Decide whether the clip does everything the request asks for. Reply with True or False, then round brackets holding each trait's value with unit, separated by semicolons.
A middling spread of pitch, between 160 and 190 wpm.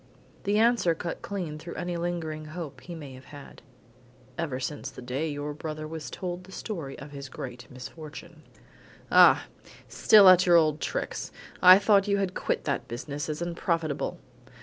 True (3.5 semitones; 170 wpm)